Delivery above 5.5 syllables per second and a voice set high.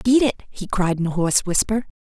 Yes: 5.7 syllables/s; high, 200 Hz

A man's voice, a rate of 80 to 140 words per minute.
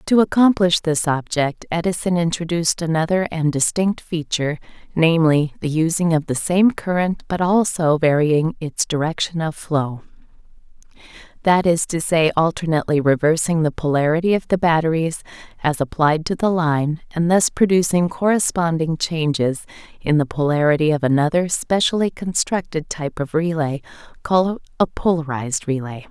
No: female; slow, 135 wpm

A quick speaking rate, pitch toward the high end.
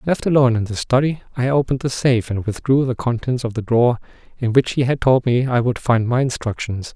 No: fast, 235 wpm; low, 125 Hz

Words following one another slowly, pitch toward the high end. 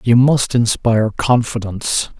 No: slow, 110 wpm; low, 115 Hz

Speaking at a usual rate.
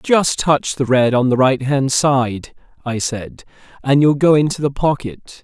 Yes: average, 175 wpm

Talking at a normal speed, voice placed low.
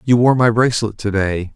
No: fast, 230 wpm; low, 110 Hz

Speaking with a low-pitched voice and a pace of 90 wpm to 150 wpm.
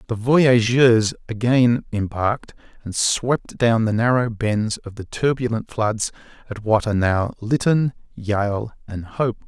Yes: low, 115 Hz; average, 140 wpm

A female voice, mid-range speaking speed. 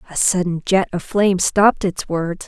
Yes: female; average, 195 wpm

